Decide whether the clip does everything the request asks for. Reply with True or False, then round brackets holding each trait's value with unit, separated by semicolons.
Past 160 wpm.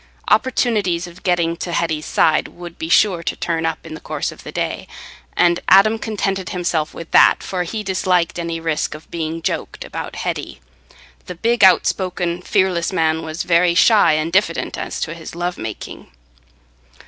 True (170 wpm)